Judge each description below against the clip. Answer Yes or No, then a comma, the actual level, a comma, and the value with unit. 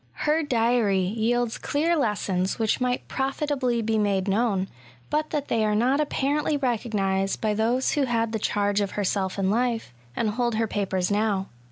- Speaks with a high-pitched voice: Yes, high, 225 Hz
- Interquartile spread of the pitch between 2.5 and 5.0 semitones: Yes, average, 3.7 semitones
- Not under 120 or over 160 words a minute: No, average, 170 wpm